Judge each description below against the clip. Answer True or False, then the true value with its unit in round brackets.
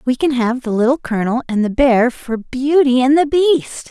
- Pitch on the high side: True (260 Hz)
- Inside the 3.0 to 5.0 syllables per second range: True (4.8 syllables/s)